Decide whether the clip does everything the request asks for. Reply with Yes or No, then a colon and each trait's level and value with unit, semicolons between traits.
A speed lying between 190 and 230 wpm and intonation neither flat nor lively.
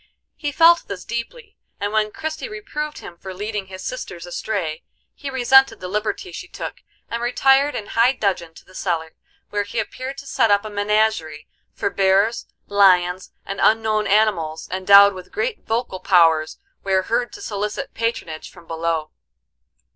No: average, 160 wpm; average, 4.7 semitones